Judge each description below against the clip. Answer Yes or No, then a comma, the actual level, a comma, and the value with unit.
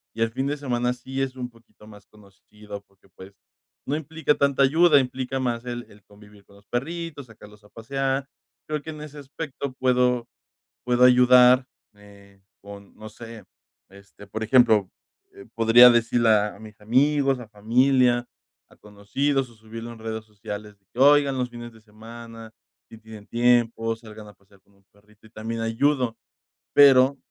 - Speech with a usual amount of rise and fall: Yes, average, 3.7 semitones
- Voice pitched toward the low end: Yes, low, 115 Hz